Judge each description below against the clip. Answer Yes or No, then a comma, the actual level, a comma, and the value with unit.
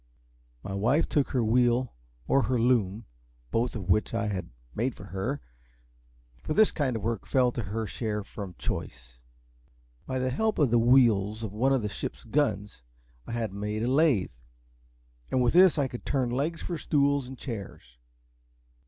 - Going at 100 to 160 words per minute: No, average, 175 wpm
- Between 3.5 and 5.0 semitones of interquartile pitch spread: Yes, average, 4.1 semitones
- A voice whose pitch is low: Yes, low, 120 Hz